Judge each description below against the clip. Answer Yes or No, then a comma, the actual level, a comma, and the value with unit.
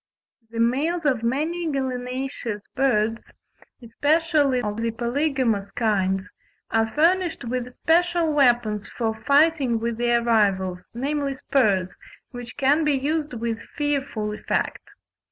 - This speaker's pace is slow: Yes, slow, 120 wpm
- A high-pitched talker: Yes, very high, 250 Hz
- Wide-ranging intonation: No, average, 4.6 semitones